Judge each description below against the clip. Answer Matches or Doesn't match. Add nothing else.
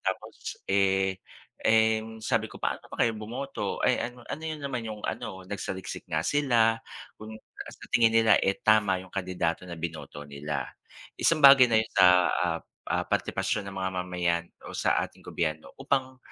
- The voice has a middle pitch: Doesn't match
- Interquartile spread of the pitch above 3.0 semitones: Matches